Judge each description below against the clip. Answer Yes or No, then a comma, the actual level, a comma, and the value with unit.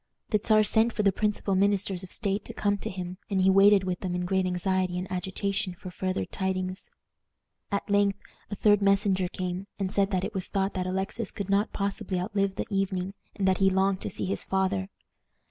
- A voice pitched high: Yes, high, 195 Hz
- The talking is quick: Yes, fast, 210 wpm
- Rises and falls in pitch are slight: Yes, narrow, 1.3 semitones